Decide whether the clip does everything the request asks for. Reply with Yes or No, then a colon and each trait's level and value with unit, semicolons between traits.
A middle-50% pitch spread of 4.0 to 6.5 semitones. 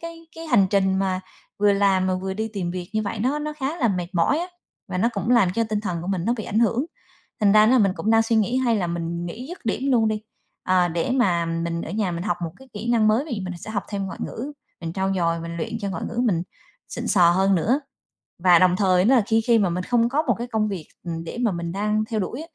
Yes: average, 4.4 semitones